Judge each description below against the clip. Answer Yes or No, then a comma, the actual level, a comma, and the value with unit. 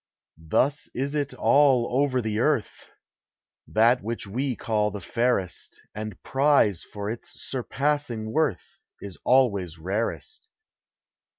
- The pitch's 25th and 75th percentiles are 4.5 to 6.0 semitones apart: Yes, average, 4.8 semitones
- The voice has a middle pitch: No, low, 120 Hz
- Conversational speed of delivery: No, slow, 115 wpm